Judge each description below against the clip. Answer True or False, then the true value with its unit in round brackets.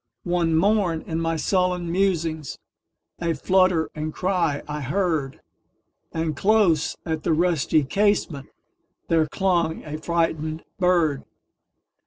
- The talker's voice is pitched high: False (165 Hz)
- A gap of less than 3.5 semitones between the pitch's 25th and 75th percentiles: True (2.7 semitones)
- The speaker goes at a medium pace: False (100 wpm)